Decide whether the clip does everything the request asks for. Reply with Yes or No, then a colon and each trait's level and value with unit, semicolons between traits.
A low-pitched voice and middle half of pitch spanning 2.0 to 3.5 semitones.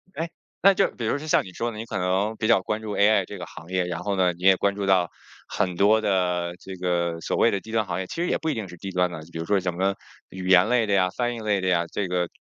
Yes: very low, 95 Hz; average, 3.2 semitones